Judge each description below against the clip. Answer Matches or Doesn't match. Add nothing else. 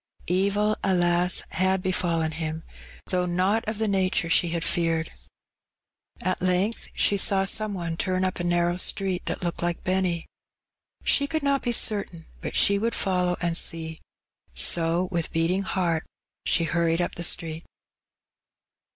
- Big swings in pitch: Doesn't match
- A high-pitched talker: Doesn't match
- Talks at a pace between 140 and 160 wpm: Matches